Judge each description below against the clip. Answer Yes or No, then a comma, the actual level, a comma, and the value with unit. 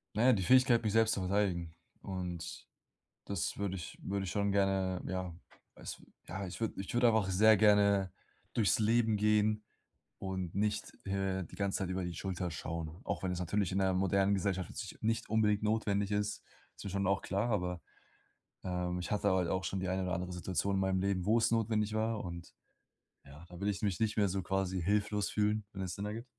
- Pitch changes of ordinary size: No, narrow, 2.3 semitones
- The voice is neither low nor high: No, low, 100 Hz